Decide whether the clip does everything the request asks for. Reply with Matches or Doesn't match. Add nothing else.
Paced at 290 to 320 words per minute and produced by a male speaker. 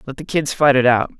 Matches